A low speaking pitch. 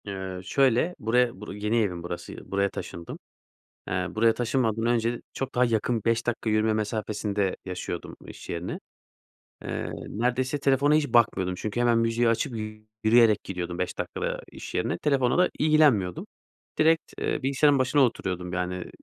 Yes: low, 115 Hz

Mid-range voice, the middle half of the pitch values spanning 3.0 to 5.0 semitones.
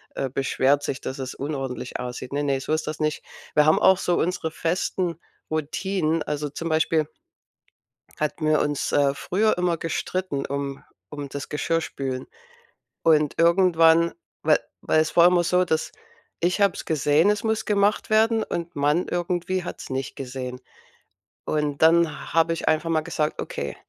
Yes: medium, 155 Hz; average, 3.4 semitones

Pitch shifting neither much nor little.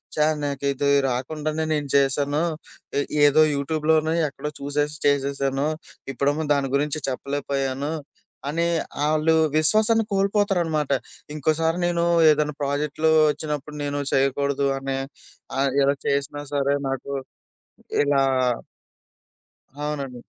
No: narrow, 2.0 semitones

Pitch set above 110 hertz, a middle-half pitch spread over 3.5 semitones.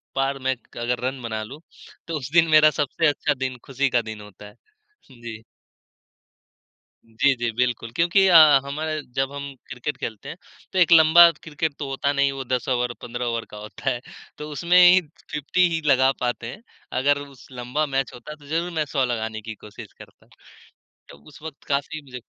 Yes: low, 135 Hz; average, 4.0 semitones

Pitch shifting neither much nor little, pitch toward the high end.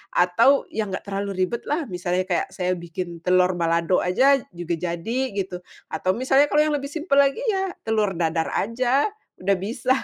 No: wide, 6.9 semitones; high, 195 Hz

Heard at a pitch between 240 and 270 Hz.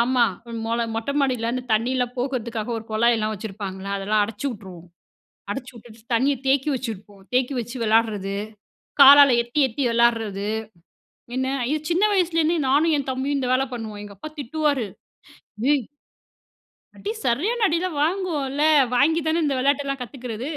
Yes: very high, 250 Hz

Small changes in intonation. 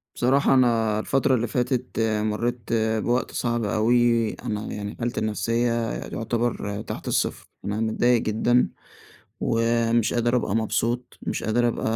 Yes: narrow, 1.7 semitones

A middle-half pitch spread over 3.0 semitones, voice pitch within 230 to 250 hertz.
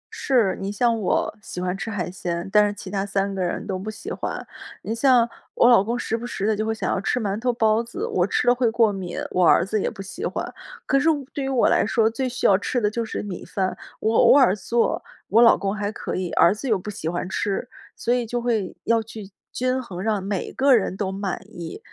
No: average, 3.5 semitones; high, 215 Hz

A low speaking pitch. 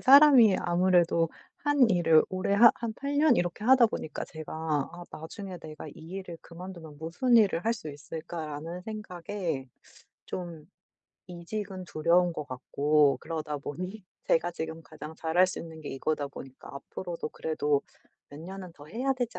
No: medium, 175 Hz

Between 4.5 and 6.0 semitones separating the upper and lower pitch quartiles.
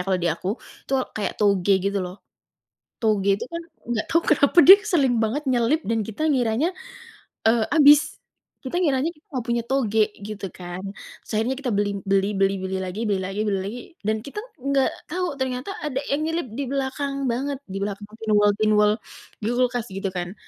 Yes: wide, 5.5 semitones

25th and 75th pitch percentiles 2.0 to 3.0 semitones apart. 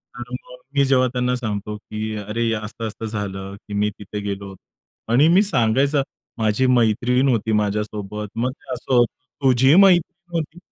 No: average, 3.9 semitones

